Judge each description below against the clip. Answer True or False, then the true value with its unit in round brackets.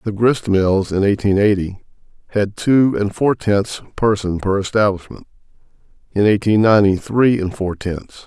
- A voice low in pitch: True (100 Hz)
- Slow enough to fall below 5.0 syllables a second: True (4.6 syllables/s)